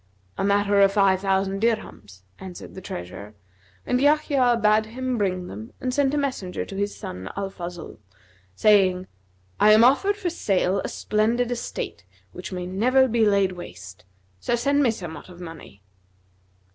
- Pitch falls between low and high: No, high, 200 Hz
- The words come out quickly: No, average, 160 wpm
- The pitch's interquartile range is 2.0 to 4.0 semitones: No, average, 4.8 semitones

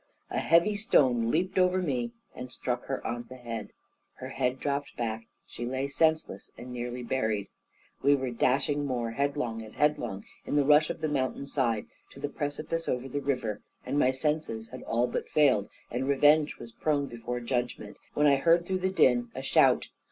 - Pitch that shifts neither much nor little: Yes, average, 3.6 semitones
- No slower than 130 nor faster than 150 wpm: No, average, 190 wpm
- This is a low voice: Yes, low, 130 Hz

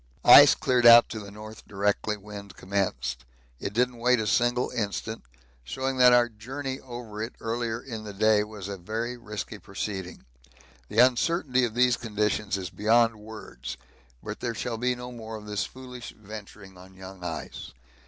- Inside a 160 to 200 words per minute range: Yes, average, 170 wpm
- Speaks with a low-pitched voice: Yes, low, 110 Hz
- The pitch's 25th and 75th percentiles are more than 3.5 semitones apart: No, average, 3.1 semitones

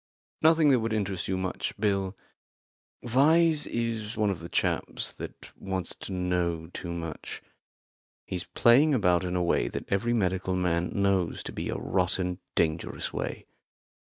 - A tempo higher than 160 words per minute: No, average, 155 wpm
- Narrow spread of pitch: No, average, 4.2 semitones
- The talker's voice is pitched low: Yes, very low, 95 Hz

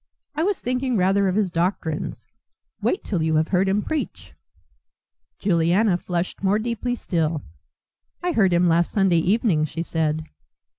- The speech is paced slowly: No, average, 150 wpm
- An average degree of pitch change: Yes, average, 4.5 semitones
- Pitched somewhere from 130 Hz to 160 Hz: No, medium, 185 Hz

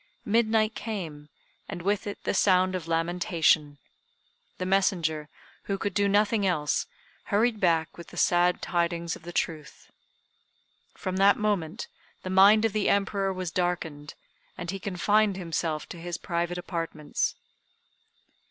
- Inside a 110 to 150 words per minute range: Yes, average, 140 wpm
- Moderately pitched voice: Yes, medium, 180 Hz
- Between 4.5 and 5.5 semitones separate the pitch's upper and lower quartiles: No, average, 3.2 semitones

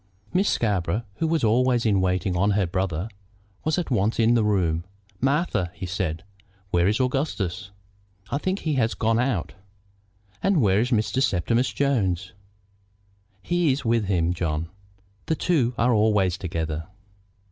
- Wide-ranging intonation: Yes, wide, 5.8 semitones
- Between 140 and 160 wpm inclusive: Yes, average, 150 wpm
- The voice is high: No, low, 105 Hz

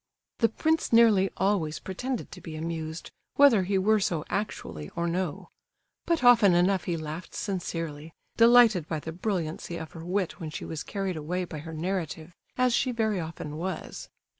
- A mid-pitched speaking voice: Yes, medium, 180 Hz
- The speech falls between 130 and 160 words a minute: No, average, 170 wpm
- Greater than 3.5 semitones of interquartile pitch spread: Yes, average, 4.5 semitones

